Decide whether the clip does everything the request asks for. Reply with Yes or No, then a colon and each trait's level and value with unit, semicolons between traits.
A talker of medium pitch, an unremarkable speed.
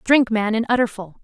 No: high, 225 Hz; average, 195 wpm